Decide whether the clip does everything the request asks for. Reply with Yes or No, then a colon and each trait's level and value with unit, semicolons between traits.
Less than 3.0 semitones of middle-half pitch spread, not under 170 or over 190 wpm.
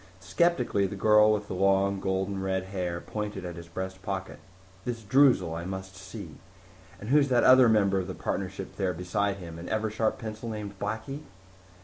Yes: narrow, 2.4 semitones; average, 180 wpm